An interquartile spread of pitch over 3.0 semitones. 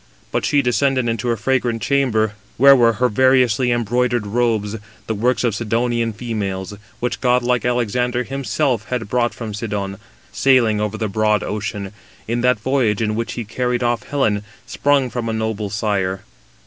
No: average, 2.7 semitones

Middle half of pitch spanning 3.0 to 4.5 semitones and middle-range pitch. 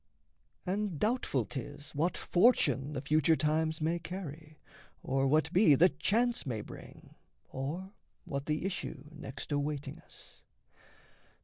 Yes: average, 4.0 semitones; medium, 155 Hz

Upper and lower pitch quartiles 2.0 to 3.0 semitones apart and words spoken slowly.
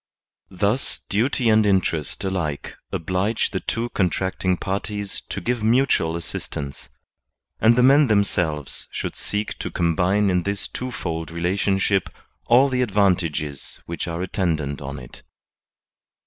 No: average, 4.4 semitones; slow, 130 wpm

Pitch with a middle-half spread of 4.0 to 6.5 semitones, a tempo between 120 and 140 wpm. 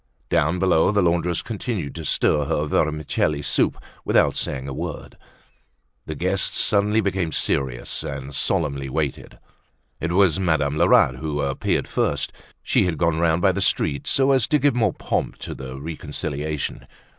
No: average, 4.5 semitones; average, 155 wpm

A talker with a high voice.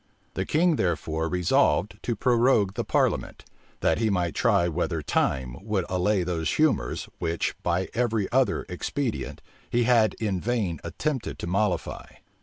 No: very low, 95 Hz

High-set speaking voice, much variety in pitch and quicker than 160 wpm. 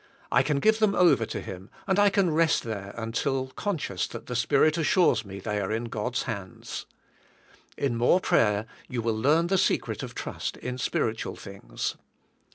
No: low, 120 Hz; wide, 7.1 semitones; average, 175 wpm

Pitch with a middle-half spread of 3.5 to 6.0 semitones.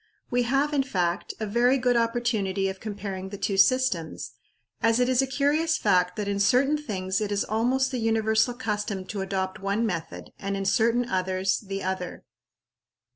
Yes: average, 4.2 semitones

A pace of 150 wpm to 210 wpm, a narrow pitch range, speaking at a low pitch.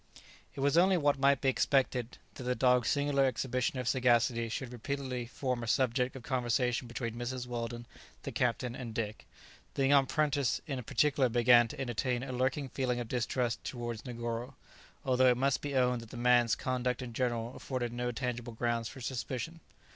Yes: average, 180 wpm; narrow, 1.9 semitones; low, 125 Hz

